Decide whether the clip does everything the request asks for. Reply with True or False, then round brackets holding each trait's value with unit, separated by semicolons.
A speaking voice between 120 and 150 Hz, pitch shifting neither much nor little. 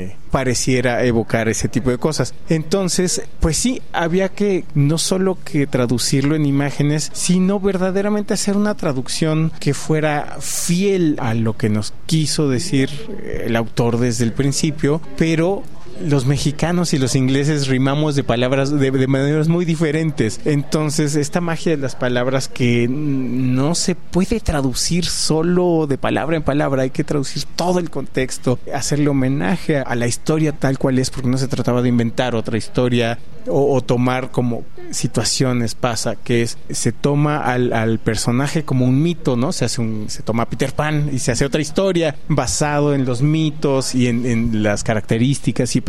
True (140 Hz; 4.0 semitones)